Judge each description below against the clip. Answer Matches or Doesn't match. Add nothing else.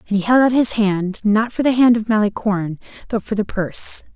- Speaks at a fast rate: Matches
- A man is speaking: Doesn't match